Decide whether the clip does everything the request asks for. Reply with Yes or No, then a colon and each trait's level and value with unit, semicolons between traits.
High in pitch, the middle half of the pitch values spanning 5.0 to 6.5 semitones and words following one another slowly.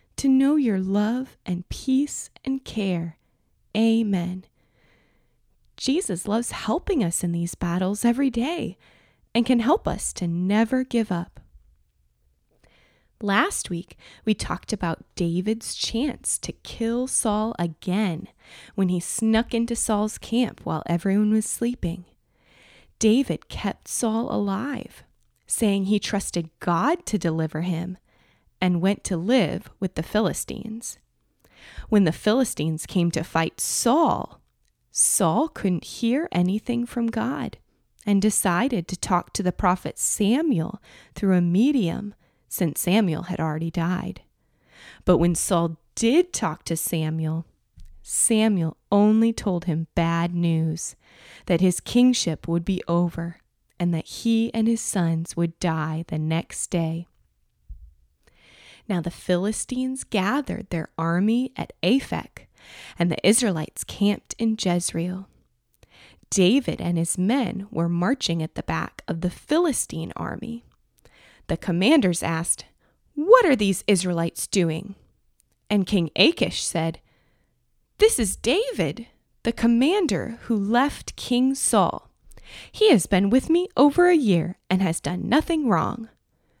Yes: high, 195 Hz; wide, 5.4 semitones; slow, 130 wpm